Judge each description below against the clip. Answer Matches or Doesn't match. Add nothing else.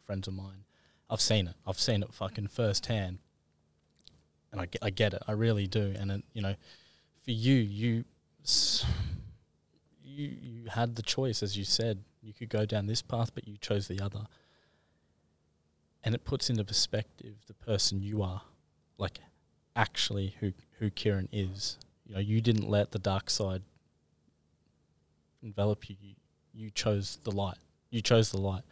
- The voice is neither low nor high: Doesn't match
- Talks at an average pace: Matches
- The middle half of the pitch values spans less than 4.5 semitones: Doesn't match